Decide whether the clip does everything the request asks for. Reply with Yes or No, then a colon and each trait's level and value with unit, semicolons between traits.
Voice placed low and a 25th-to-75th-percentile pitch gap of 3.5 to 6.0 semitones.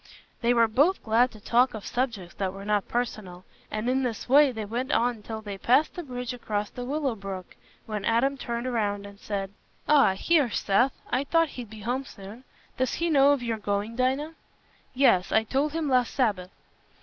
No: high, 235 Hz; average, 4.1 semitones